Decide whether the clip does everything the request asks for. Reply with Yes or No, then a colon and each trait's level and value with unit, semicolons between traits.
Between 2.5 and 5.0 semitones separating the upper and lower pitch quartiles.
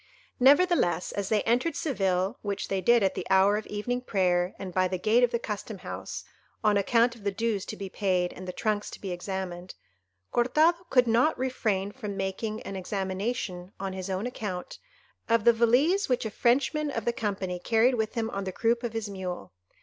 Yes: average, 4.0 semitones